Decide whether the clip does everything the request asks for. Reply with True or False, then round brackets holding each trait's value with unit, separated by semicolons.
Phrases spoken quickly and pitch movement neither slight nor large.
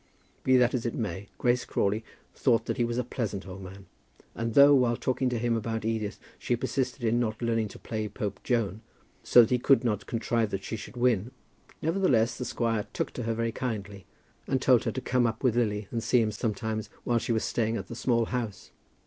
False (220 wpm; 2.1 semitones)